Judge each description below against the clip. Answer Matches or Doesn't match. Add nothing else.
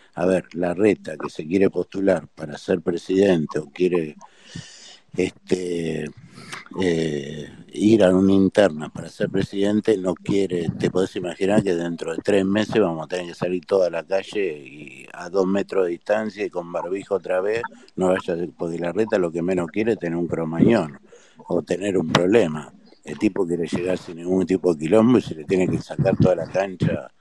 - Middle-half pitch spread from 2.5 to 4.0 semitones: Matches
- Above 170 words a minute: Matches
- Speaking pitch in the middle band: Doesn't match